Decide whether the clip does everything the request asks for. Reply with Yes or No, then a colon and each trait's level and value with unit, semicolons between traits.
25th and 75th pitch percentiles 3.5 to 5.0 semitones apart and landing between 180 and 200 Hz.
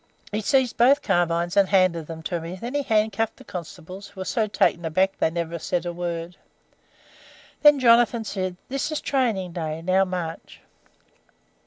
Yes: average, 4.7 semitones; medium, 185 Hz